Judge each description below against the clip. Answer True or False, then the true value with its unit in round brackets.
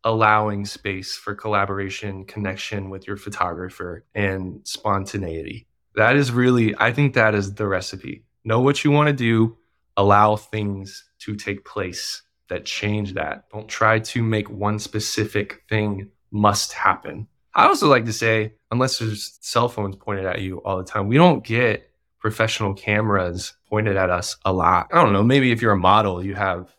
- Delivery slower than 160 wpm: False (175 wpm)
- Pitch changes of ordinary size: False (2.2 semitones)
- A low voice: True (105 Hz)